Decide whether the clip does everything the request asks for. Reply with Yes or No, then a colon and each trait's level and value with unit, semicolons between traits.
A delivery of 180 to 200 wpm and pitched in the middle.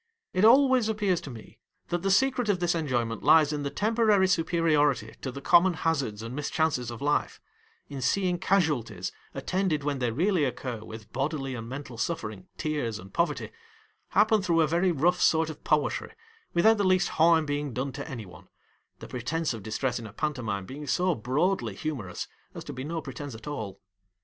Yes: average, 190 wpm; medium, 150 Hz